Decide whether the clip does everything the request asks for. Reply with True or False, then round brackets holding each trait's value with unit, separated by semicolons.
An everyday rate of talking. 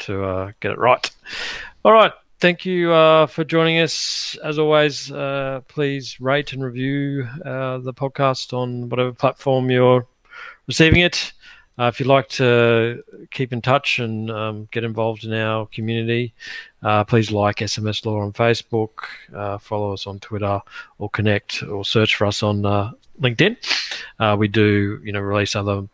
True (165 wpm)